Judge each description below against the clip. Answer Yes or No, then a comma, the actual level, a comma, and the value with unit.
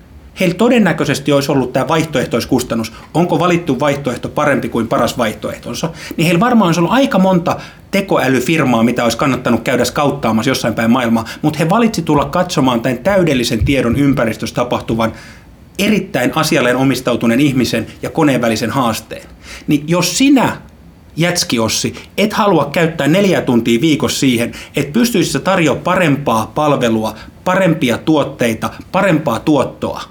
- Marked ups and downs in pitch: Yes, wide, 6.4 semitones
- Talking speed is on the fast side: No, average, 135 wpm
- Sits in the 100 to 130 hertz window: No, medium, 140 Hz